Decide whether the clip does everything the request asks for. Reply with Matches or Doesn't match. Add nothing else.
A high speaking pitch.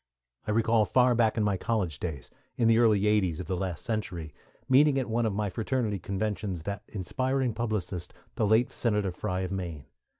Doesn't match